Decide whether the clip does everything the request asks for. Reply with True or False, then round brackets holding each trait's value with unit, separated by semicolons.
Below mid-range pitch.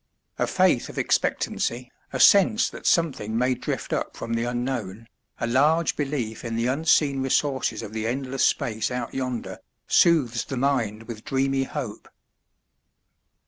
True (125 Hz)